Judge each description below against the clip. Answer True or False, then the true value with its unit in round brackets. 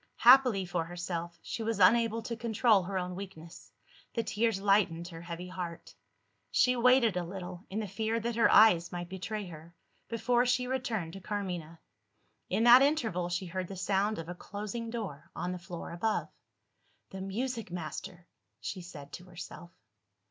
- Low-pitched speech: False (190 Hz)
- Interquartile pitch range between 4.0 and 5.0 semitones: True (4.5 semitones)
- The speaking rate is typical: True (170 wpm)